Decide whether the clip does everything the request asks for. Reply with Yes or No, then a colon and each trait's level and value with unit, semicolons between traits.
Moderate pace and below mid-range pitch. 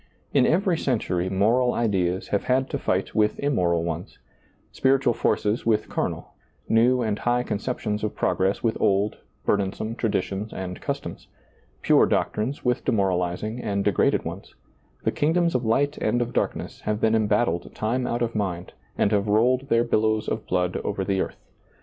Yes: average, 160 wpm; low, 110 Hz